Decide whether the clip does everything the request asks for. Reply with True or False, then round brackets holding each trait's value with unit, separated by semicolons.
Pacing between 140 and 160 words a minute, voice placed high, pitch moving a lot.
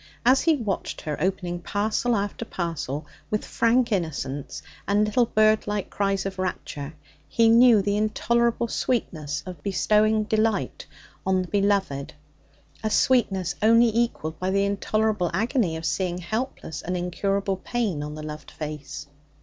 False (145 wpm; 200 Hz; 4.1 semitones)